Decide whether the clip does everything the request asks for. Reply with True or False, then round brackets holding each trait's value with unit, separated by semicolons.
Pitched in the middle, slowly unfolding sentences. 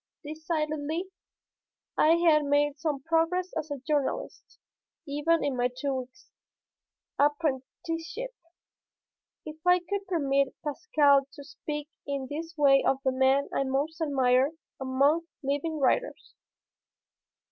False (295 Hz; 115 wpm)